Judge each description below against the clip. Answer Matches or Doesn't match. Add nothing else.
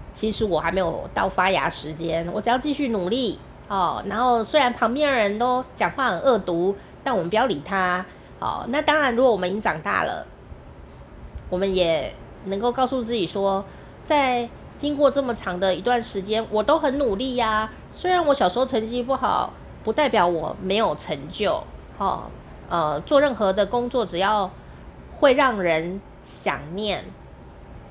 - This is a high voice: Matches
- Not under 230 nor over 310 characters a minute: Matches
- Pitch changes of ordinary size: Doesn't match